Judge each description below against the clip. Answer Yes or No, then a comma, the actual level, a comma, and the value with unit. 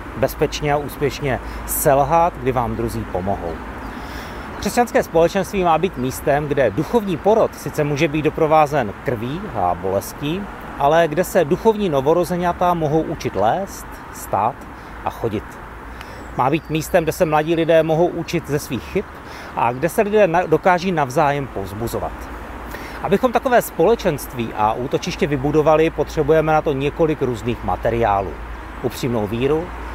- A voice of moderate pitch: Yes, medium, 155 Hz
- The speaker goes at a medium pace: Yes, average, 135 wpm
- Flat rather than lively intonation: No, wide, 6.4 semitones